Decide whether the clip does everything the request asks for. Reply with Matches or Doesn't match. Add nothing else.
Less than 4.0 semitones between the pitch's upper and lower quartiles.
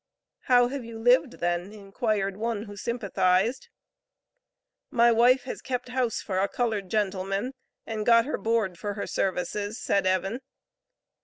Matches